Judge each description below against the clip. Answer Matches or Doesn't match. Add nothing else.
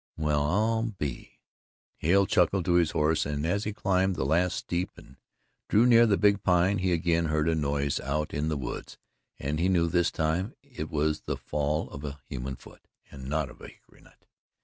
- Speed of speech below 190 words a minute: Doesn't match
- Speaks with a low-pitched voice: Matches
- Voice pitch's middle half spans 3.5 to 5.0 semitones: Matches